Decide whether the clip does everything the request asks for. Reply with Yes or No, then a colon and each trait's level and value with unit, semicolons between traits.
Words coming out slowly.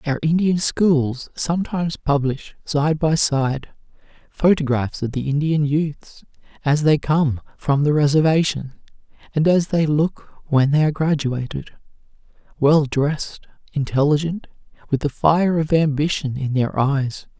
Yes: slow, 130 wpm